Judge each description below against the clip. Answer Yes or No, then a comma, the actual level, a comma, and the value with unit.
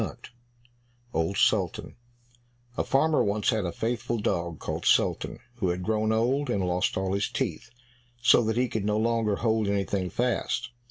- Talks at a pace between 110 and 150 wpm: No, average, 165 wpm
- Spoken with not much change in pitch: No, average, 3.4 semitones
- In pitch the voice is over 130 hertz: No, low, 110 Hz